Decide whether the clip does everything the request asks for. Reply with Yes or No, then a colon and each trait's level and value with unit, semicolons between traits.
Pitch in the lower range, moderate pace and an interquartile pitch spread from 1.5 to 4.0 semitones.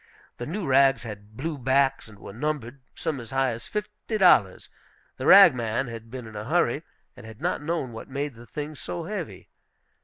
No: low, 130 Hz; average, 195 wpm; average, 4.7 semitones